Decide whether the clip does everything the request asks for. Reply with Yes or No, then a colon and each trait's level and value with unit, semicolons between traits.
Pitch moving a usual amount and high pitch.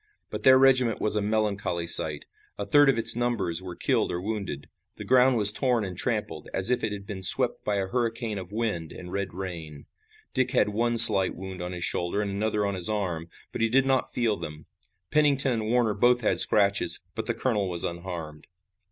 No: average, 4.6 semitones; low, 105 Hz